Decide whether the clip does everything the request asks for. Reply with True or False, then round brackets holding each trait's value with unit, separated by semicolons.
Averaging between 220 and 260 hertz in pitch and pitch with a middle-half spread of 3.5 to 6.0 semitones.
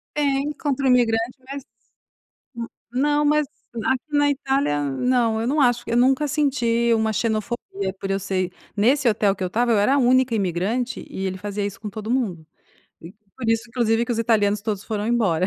True (230 Hz; 4.2 semitones)